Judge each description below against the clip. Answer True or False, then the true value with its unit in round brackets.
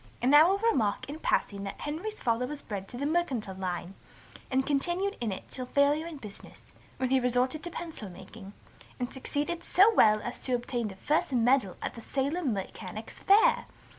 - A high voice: True (260 Hz)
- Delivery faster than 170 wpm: True (195 wpm)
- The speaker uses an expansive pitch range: True (6.1 semitones)